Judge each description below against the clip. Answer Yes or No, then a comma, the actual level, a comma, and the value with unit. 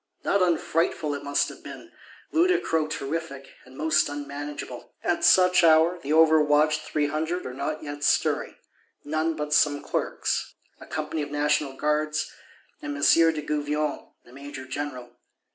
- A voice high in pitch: No, medium, 150 Hz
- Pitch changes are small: Yes, narrow, 2.0 semitones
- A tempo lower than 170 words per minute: Yes, average, 145 wpm